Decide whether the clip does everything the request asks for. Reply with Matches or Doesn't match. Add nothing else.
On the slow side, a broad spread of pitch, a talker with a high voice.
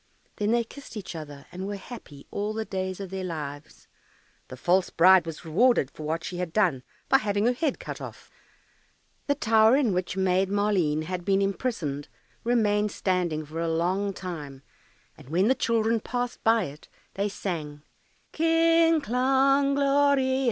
Doesn't match